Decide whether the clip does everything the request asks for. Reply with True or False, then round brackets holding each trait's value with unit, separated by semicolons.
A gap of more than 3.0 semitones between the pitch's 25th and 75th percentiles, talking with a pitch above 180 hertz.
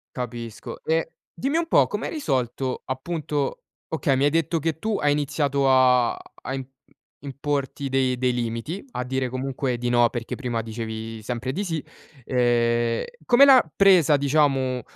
False (3.7 semitones; 135 Hz)